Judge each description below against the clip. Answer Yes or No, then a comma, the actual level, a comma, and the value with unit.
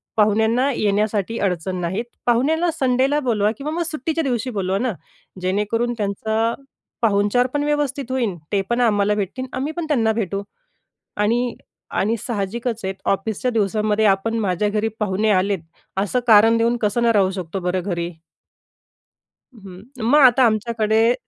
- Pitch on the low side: No, high, 220 Hz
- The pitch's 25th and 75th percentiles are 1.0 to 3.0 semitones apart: No, average, 3.5 semitones